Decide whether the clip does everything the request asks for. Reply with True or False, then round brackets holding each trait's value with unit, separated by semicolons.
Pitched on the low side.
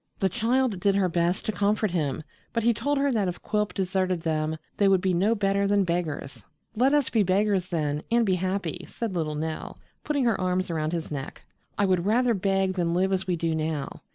False (190 Hz)